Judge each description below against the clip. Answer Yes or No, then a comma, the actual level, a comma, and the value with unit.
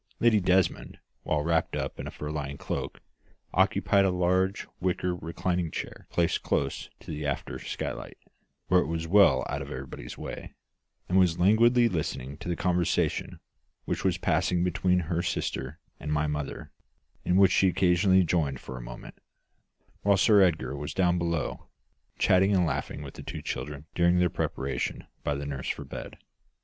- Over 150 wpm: Yes, average, 170 wpm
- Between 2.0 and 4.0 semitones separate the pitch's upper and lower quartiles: Yes, average, 3.7 semitones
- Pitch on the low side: Yes, very low, 85 Hz